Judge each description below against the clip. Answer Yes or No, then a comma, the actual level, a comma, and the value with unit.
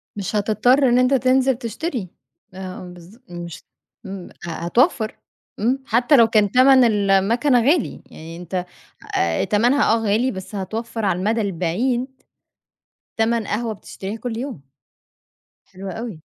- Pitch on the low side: No, high, 220 Hz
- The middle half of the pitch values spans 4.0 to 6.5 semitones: Yes, average, 4.6 semitones